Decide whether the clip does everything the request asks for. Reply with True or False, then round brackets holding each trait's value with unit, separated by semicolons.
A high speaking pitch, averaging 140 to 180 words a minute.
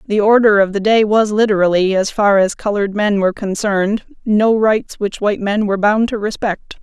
False (205 Hz; 200 wpm)